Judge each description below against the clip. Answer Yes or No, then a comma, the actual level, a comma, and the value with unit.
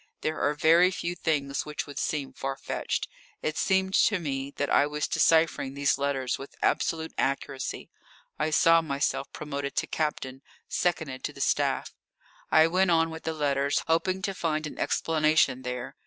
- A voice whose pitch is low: No, medium, 150 Hz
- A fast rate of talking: No, average, 170 wpm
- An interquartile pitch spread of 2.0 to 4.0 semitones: Yes, average, 2.8 semitones